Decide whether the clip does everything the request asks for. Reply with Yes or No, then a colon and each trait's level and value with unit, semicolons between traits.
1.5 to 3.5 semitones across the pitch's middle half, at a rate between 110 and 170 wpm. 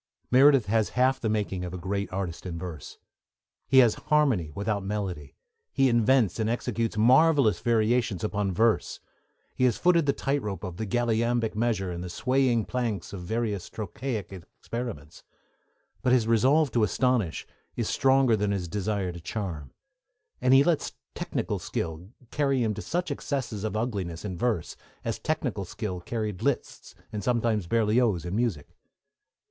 No: average, 4.4 semitones; average, 160 wpm